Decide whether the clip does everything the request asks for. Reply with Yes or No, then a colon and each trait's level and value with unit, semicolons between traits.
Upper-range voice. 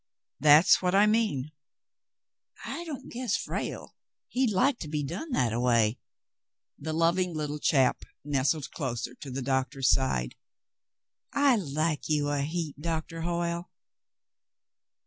No: medium, 155 Hz